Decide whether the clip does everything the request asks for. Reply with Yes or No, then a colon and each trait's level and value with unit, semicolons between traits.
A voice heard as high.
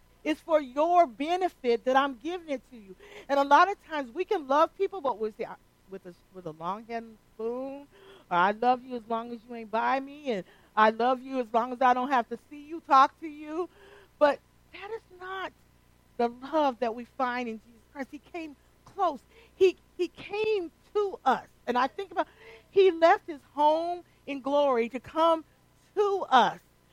Yes: very high, 280 Hz